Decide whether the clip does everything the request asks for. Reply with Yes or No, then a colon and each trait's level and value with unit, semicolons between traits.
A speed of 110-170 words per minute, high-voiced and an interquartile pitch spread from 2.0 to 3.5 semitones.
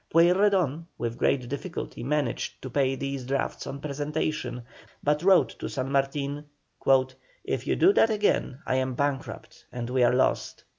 No: average, 160 wpm; medium, 140 Hz; average, 2.8 semitones